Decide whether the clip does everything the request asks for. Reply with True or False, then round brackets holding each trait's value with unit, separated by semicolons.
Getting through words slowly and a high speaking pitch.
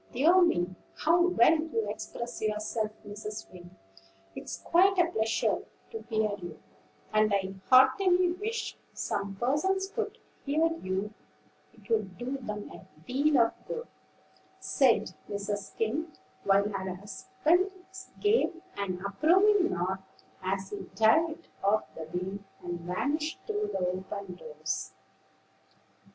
True (125 wpm; 220 Hz)